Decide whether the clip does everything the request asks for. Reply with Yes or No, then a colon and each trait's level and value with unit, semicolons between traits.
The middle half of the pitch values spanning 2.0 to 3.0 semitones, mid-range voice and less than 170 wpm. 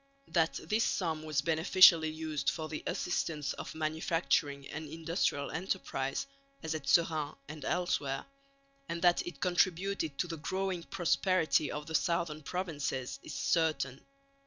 Yes: narrow, 2.6 semitones; medium, 160 Hz; slow, 135 wpm